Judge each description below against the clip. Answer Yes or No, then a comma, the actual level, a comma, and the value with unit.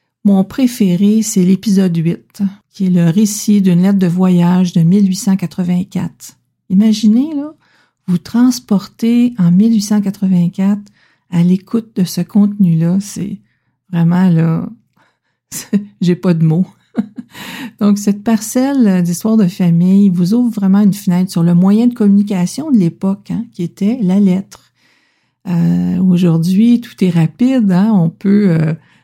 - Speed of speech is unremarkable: No, slow, 135 wpm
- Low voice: No, high, 195 Hz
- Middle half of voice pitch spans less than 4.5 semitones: Yes, average, 3.1 semitones